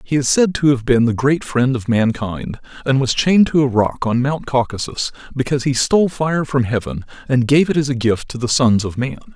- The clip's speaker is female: No, male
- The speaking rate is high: Yes, fast, 235 wpm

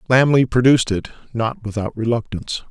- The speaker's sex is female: No, male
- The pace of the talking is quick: No, slow, 135 wpm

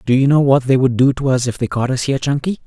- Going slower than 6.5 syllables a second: No, 6.8 syllables/s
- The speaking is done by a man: Yes, male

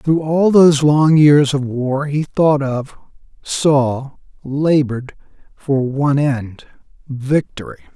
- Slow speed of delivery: Yes, slow, 115 wpm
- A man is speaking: Yes, male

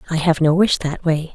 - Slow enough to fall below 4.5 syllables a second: No, 5.3 syllables/s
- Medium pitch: Yes, medium, 165 Hz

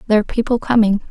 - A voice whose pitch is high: Yes, high, 220 Hz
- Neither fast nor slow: No, fast, 215 wpm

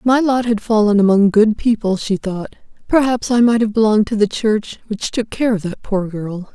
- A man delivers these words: No, female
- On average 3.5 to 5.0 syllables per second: No, 5.2 syllables/s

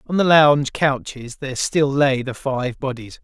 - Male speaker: Yes, male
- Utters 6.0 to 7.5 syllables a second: No, 4.6 syllables/s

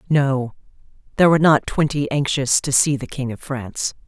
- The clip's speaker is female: Yes, female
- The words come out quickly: No, average, 175 wpm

